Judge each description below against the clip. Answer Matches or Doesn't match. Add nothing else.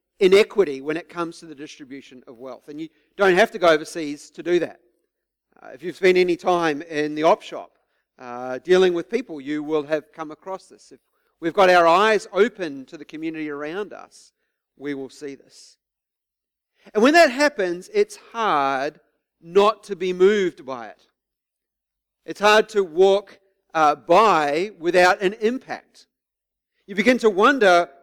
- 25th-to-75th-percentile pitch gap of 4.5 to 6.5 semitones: Matches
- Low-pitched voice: Doesn't match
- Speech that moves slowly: Doesn't match